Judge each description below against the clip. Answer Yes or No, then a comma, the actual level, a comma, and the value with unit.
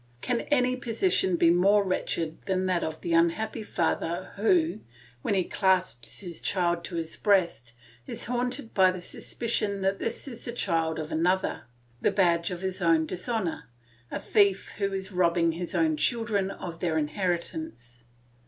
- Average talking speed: Yes, average, 160 wpm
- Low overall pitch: No, medium, 185 Hz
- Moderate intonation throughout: Yes, average, 3.6 semitones